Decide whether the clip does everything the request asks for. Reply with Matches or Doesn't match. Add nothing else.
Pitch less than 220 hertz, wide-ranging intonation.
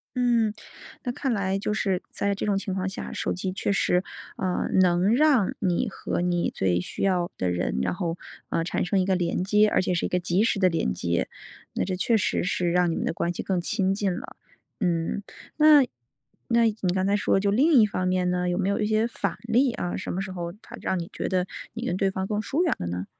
Doesn't match